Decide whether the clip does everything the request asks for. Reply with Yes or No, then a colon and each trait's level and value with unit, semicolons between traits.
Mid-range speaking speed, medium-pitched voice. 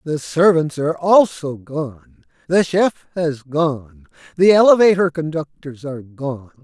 No: slow, 125 wpm; medium, 155 Hz